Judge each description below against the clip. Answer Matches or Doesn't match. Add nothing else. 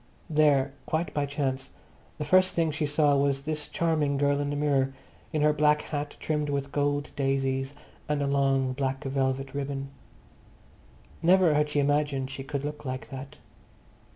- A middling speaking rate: Matches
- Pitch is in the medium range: Matches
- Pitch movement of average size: Doesn't match